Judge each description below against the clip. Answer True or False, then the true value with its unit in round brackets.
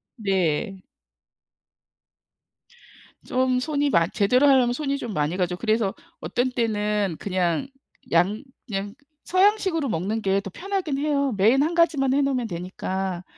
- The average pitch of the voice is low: False (225 Hz)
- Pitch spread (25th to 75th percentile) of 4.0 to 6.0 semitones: False (6.4 semitones)